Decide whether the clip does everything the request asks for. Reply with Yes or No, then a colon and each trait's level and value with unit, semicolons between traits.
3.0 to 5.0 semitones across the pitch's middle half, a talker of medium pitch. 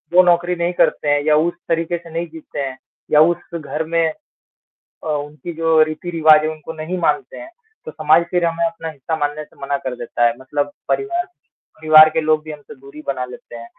No: narrow, 2.4 semitones; medium, 155 Hz